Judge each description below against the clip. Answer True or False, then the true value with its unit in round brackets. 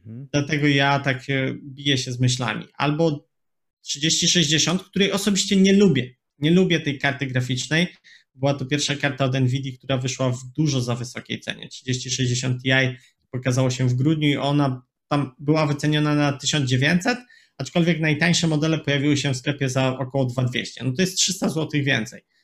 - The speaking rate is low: False (160 wpm)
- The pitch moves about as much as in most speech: True (3.4 semitones)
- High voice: False (140 Hz)